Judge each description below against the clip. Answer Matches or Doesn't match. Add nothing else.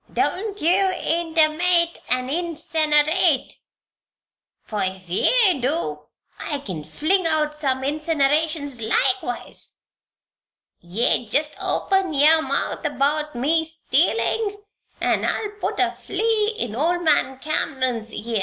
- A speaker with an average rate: Doesn't match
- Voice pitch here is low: Doesn't match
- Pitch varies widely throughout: Doesn't match